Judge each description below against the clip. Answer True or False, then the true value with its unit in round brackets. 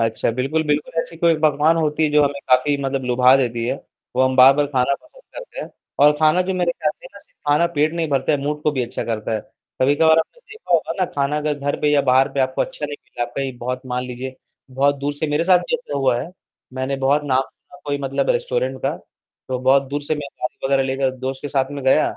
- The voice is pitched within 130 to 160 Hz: True (140 Hz)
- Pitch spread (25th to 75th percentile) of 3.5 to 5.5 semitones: False (2.7 semitones)